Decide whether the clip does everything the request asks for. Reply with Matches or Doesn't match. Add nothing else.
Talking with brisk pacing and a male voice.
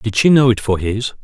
Matches